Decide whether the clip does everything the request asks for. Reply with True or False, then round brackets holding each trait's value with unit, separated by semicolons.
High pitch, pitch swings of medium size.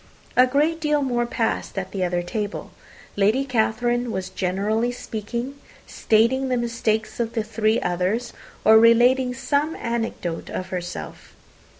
True (230 Hz; 3.2 semitones)